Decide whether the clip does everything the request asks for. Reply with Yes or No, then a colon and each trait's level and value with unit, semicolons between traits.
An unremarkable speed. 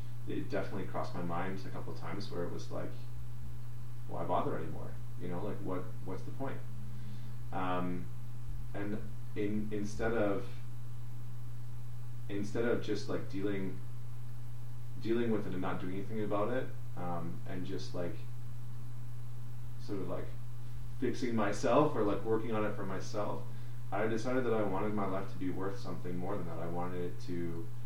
Yes: average, 165 wpm